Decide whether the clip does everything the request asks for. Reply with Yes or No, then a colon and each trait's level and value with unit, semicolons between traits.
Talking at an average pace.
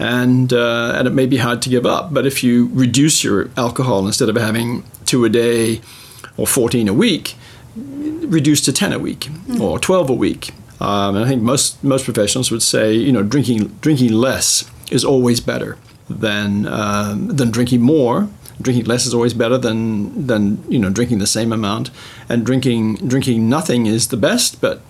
Yes: average, 190 wpm